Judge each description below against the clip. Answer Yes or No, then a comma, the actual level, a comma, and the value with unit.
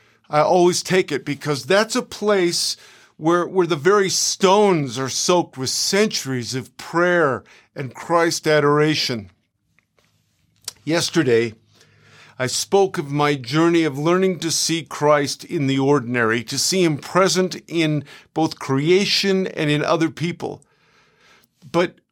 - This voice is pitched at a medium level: Yes, medium, 160 Hz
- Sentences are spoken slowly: Yes, slow, 130 wpm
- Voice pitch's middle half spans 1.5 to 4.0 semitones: No, average, 4.6 semitones